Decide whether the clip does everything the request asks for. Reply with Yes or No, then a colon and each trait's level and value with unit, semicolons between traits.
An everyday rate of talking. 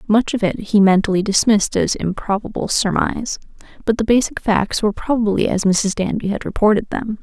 Yes: average, 175 wpm